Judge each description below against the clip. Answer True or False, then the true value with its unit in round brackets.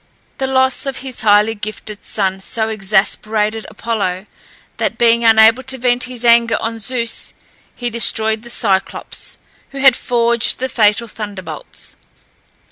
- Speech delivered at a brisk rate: False (135 wpm)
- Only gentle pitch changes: True (2.3 semitones)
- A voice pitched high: True (225 Hz)